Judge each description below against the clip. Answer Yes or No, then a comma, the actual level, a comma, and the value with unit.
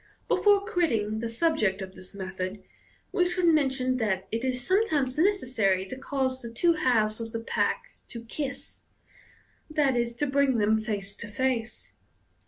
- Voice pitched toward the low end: No, high, 245 Hz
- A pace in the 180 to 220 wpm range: No, average, 160 wpm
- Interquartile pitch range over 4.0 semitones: Yes, average, 4.9 semitones